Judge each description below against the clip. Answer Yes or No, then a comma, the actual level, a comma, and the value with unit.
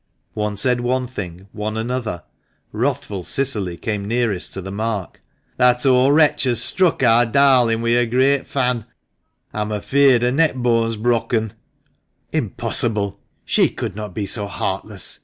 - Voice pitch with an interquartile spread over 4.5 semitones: No, average, 3.3 semitones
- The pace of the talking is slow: No, average, 150 wpm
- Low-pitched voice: Yes, low, 115 Hz